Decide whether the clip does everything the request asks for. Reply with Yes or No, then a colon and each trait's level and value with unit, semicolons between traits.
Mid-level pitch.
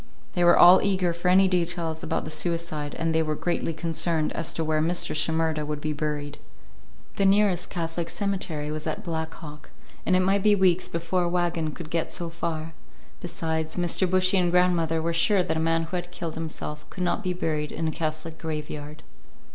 Yes: medium, 165 Hz